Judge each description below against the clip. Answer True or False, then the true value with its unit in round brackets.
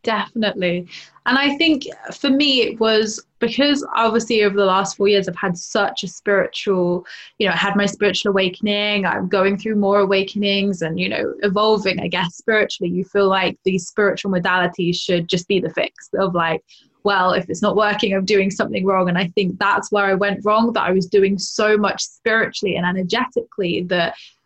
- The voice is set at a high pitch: True (200 Hz)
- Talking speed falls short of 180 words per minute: False (195 wpm)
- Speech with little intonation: True (2.3 semitones)